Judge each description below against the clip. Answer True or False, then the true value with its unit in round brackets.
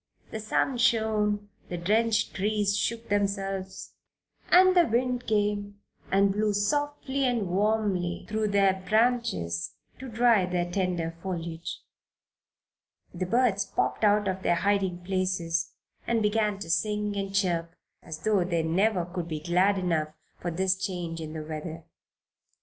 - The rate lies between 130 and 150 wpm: True (140 wpm)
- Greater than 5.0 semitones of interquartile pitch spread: False (3.5 semitones)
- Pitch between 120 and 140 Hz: False (195 Hz)